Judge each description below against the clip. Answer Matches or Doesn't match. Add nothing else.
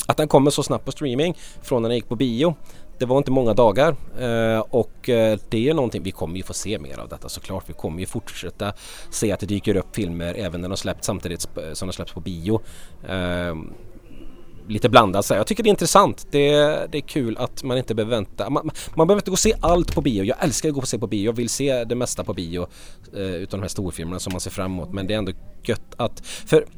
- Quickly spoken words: Matches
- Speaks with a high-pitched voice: Doesn't match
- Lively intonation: Matches